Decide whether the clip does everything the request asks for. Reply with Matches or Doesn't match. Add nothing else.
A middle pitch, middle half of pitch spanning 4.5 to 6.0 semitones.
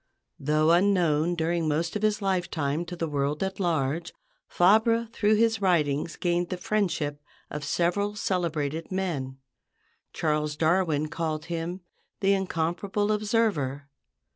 Doesn't match